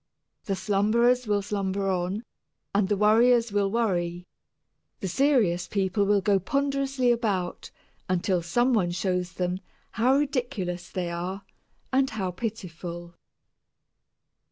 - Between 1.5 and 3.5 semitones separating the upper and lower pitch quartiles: No, average, 4.5 semitones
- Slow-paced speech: Yes, slow, 120 wpm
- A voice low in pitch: No, high, 200 Hz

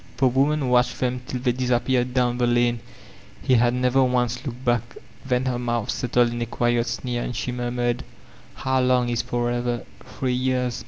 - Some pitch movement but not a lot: No, narrow, 0.9 semitones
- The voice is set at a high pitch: No, low, 125 Hz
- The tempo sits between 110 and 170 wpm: No, average, 180 wpm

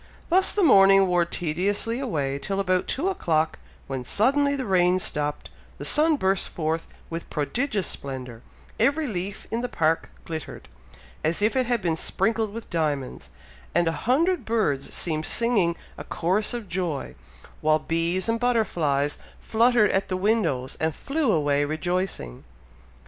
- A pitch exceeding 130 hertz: Yes, medium, 185 Hz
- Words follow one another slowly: No, average, 150 wpm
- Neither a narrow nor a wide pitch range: No, wide, 6.6 semitones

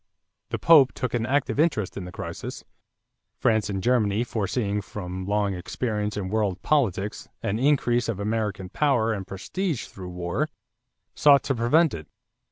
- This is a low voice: Yes, low, 110 Hz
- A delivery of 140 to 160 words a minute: Yes, average, 155 wpm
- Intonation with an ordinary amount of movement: Yes, average, 4.6 semitones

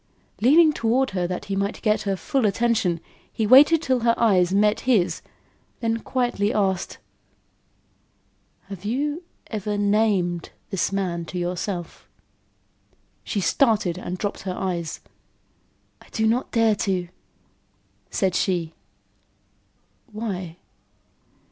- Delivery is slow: Yes, slow, 115 wpm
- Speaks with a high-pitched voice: Yes, high, 205 Hz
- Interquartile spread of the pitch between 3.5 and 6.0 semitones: Yes, average, 4.1 semitones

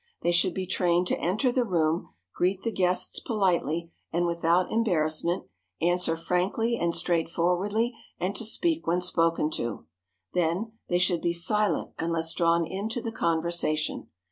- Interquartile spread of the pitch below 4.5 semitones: Yes, average, 2.8 semitones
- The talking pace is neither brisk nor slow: Yes, average, 145 wpm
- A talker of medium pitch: Yes, medium, 175 Hz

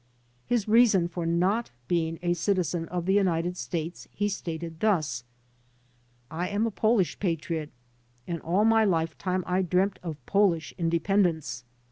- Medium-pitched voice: Yes, medium, 175 Hz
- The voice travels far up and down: No, average, 3.3 semitones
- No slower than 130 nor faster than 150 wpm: Yes, average, 140 wpm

